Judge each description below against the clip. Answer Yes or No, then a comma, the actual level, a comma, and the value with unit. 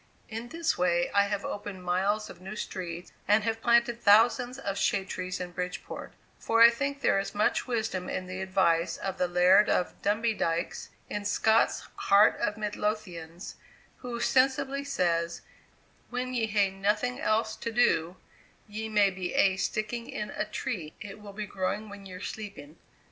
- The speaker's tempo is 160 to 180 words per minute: Yes, average, 170 wpm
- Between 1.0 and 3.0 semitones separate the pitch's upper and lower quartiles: No, average, 3.5 semitones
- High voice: Yes, high, 205 Hz